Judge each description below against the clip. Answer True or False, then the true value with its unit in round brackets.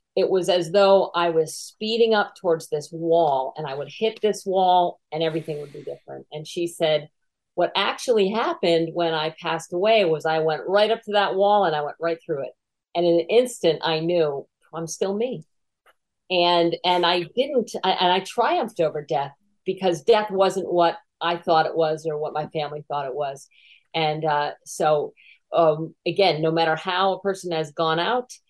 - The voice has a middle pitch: True (170 Hz)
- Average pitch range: True (3.4 semitones)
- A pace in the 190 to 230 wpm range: True (195 wpm)